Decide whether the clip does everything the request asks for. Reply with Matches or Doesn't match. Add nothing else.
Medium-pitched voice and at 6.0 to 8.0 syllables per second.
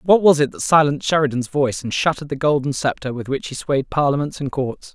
Matches